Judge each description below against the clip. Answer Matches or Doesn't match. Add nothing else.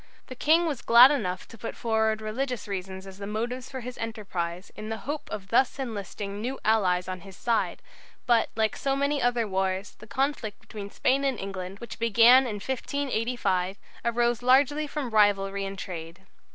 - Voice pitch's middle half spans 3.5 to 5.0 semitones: Matches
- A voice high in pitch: Matches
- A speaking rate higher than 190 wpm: Doesn't match